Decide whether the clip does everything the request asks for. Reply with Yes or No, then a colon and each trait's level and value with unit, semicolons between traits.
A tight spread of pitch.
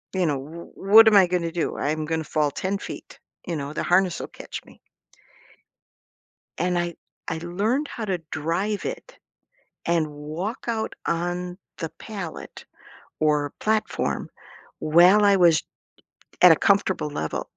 No: average, 3.9 semitones